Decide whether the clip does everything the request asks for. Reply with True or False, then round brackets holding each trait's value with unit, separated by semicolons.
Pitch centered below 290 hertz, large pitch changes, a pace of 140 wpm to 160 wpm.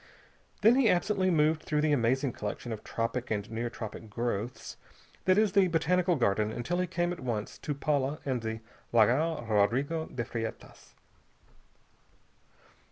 True (135 Hz; 6.9 semitones; 150 wpm)